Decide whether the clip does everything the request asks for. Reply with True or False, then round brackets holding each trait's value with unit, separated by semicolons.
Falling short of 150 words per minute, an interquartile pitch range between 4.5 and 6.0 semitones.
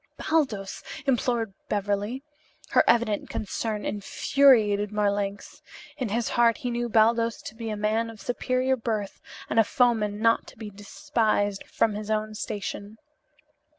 False (140 wpm; 2.4 semitones)